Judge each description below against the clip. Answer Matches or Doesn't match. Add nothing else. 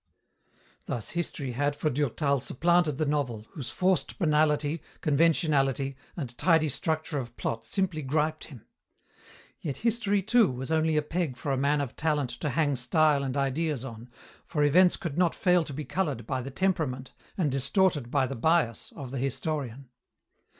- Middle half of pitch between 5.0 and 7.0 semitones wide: Doesn't match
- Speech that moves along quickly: Doesn't match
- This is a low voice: Doesn't match